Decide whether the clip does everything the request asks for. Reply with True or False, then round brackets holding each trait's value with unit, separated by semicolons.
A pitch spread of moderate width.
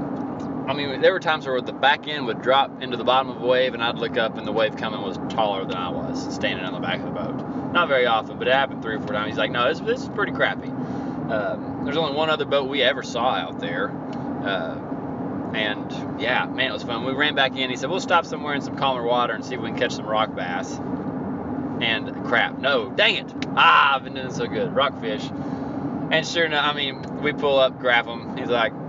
False (2.1 semitones)